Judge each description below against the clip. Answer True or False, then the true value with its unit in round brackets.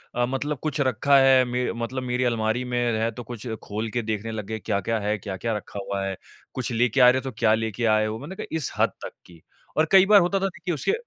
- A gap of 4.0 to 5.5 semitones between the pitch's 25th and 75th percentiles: False (3.3 semitones)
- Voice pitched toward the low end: True (120 Hz)